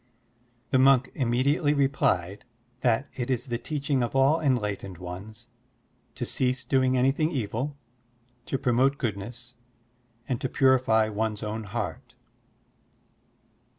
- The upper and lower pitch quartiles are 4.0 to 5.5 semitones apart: No, average, 3.5 semitones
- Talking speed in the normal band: No, slow, 115 wpm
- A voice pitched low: Yes, low, 125 Hz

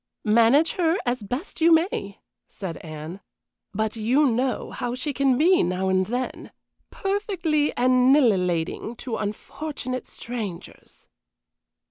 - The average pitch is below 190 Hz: No, high, 245 Hz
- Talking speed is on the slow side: Yes, slow, 115 wpm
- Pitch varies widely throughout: Yes, wide, 6.5 semitones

